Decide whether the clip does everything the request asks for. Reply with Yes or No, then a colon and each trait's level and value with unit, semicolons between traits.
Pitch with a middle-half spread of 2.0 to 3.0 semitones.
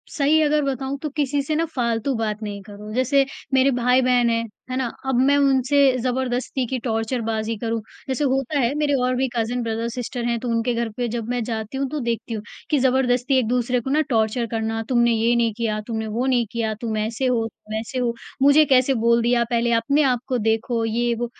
Yes: narrow, 2.6 semitones